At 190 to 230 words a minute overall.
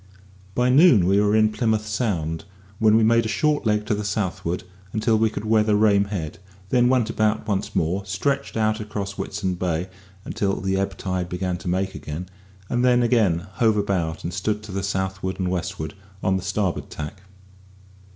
No: average, 180 wpm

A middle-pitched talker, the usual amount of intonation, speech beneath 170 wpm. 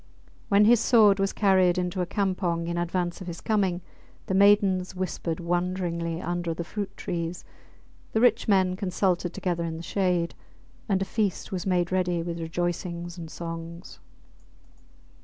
No: medium, 180 Hz; narrow, 2.1 semitones; average, 155 wpm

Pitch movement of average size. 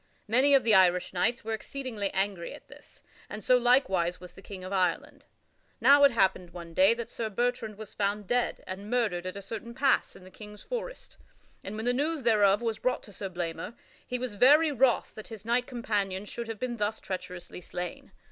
Yes: average, 4.4 semitones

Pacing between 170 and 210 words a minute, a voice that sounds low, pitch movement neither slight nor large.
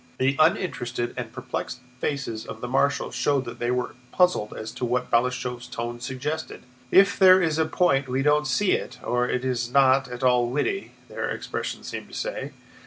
Yes: average, 185 wpm; low, 130 Hz; average, 3.5 semitones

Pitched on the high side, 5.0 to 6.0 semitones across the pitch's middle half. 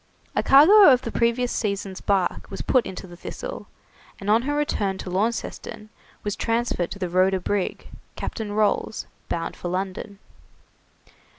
No: high, 205 Hz; average, 3.7 semitones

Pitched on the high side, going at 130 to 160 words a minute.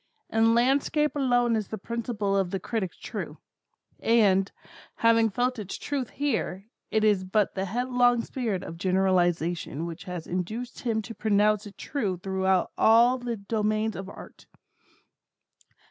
Yes: high, 215 Hz; average, 145 wpm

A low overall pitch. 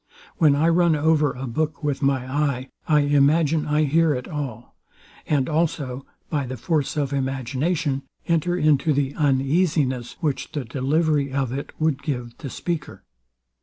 No: medium, 145 Hz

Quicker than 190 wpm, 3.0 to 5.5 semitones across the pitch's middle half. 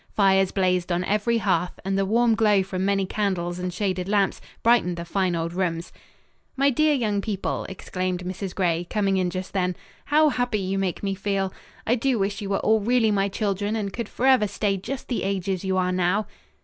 No: average, 200 wpm; narrow, 2.5 semitones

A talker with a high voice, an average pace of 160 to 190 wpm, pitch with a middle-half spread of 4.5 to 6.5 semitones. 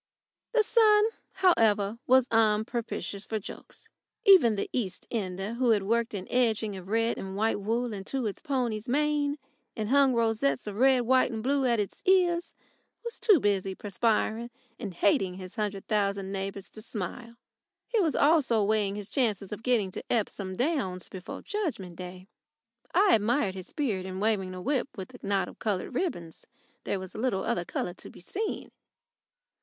Yes: high, 220 Hz; average, 170 wpm; average, 4.8 semitones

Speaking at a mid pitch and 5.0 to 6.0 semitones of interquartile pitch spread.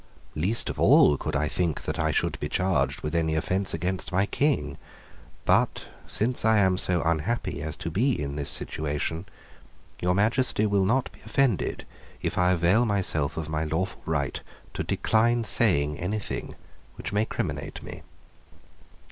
No: very low, 90 Hz; wide, 5.4 semitones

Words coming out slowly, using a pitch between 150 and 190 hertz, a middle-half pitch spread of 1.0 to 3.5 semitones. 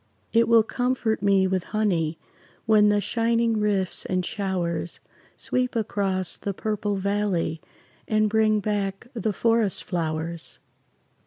No: slow, 125 wpm; high, 205 Hz; average, 2.8 semitones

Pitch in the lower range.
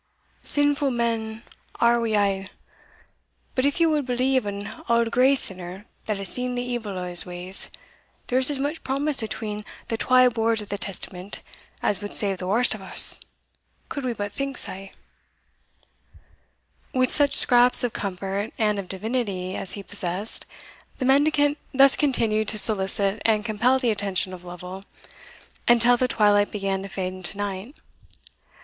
No: high, 220 Hz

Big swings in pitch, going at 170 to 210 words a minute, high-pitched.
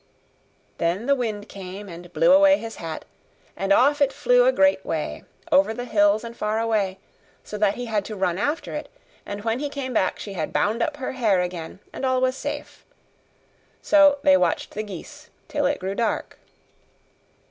Yes: wide, 5.9 semitones; average, 190 wpm; high, 225 Hz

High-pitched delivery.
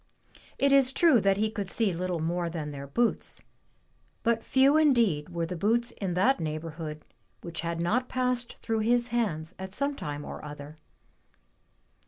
Yes: high, 195 Hz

